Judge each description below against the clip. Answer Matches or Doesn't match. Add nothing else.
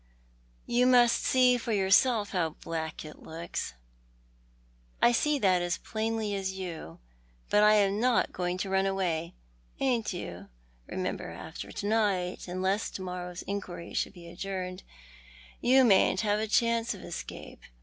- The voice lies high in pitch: Matches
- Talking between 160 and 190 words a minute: Doesn't match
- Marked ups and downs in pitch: Doesn't match